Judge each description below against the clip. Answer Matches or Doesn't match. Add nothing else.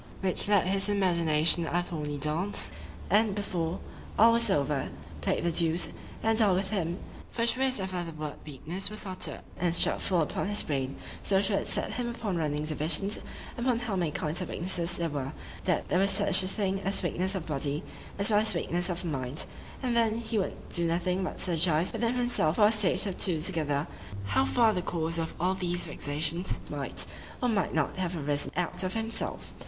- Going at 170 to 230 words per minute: Matches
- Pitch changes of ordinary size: Matches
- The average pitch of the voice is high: Doesn't match